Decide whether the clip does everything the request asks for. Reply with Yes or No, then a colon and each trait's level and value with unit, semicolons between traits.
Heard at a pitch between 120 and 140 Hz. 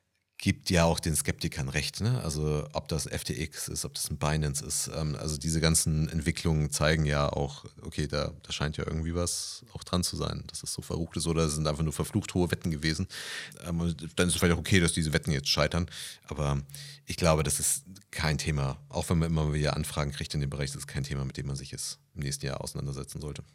No: very low, 80 Hz